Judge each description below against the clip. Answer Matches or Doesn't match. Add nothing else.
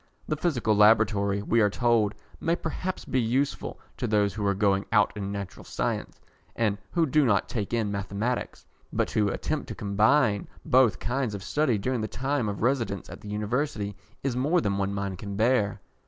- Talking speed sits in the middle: Matches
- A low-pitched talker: Matches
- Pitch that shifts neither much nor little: Matches